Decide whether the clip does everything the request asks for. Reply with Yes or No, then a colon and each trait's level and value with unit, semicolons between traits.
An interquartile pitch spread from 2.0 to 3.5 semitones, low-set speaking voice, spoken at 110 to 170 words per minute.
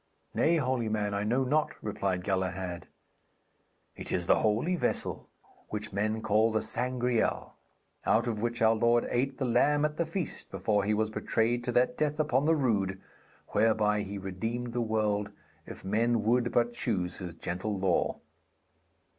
Yes: average, 3.2 semitones; low, 110 Hz; average, 165 wpm